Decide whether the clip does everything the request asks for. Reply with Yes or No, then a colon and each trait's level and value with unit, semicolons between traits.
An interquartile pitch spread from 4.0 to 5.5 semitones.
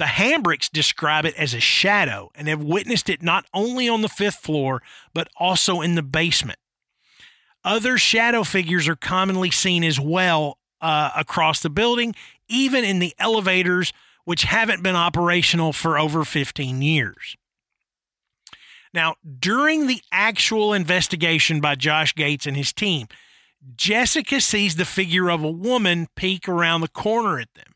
Yes: average, 4.8 semitones